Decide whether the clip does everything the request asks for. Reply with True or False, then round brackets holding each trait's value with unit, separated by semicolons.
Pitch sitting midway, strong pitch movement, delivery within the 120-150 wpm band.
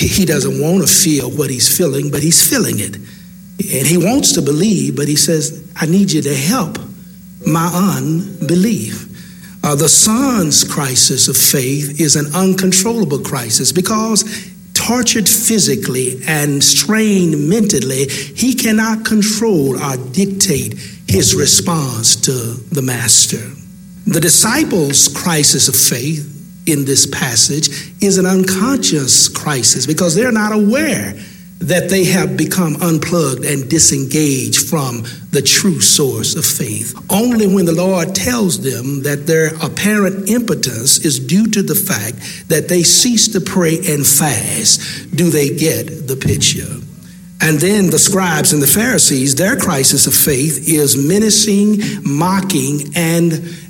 False (165 Hz; 4.9 semitones; 140 wpm)